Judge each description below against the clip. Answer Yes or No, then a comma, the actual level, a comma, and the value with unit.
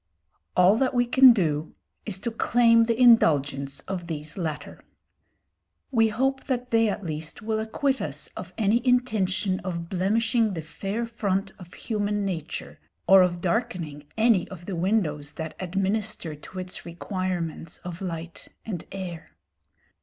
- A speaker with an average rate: Yes, average, 145 wpm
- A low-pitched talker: No, high, 190 Hz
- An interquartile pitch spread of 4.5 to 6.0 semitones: Yes, average, 4.9 semitones